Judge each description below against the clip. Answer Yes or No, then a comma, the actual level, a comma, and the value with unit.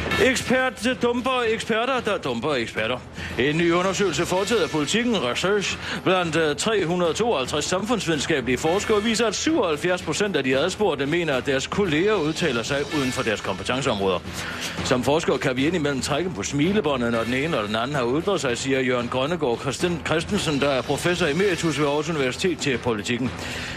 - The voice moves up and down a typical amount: No, wide, 6.9 semitones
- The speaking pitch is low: No, medium, 160 Hz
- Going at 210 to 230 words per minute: No, average, 165 wpm